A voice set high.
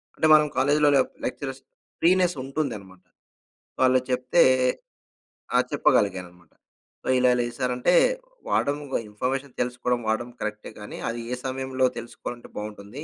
No: low, 125 Hz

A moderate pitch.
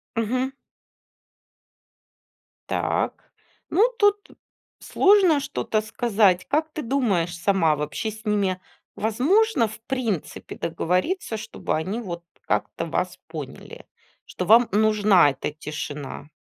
No: high, 215 Hz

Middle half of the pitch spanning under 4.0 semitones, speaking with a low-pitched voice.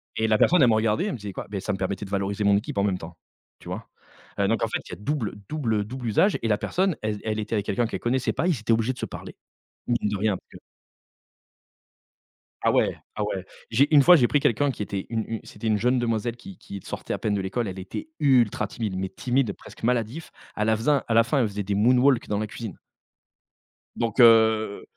Yes: average, 3.5 semitones; low, 110 Hz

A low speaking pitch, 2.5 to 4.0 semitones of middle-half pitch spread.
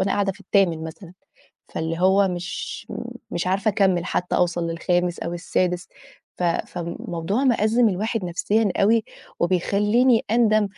No: high, 190 Hz; average, 3.4 semitones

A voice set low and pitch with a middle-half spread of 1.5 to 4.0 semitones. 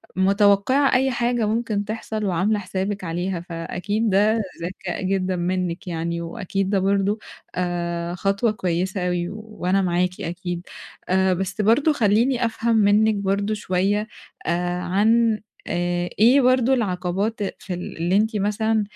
No: high, 195 Hz; average, 3.4 semitones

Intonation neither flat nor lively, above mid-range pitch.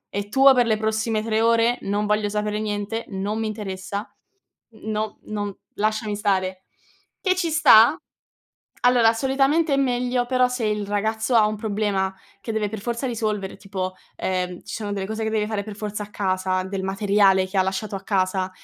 No: narrow, 2.2 semitones; high, 210 Hz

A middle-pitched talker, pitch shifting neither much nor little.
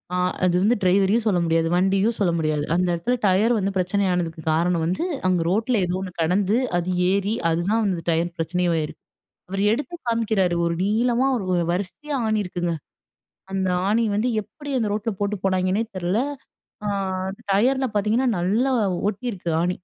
No: high, 195 Hz; average, 3.7 semitones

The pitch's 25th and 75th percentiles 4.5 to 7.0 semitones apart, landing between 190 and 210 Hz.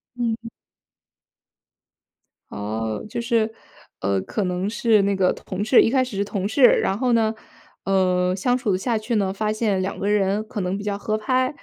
No: average, 3.1 semitones; high, 205 Hz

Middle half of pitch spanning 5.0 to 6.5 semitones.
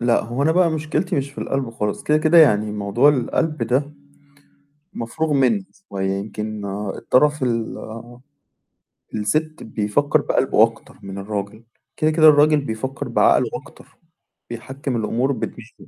Yes: wide, 5.5 semitones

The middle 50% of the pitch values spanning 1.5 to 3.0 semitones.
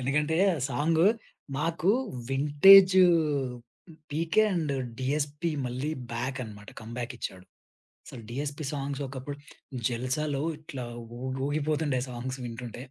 No: average, 3.4 semitones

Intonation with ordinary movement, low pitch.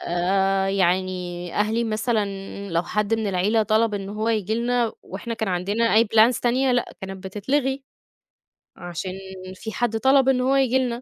No: average, 3.7 semitones; high, 215 Hz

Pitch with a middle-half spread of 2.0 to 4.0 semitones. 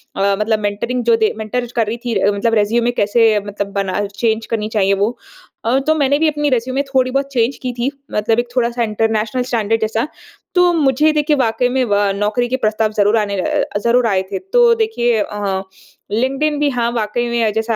Yes: average, 3.3 semitones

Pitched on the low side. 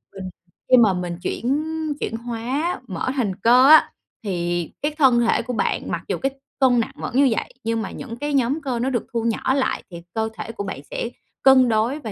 No: high, 235 Hz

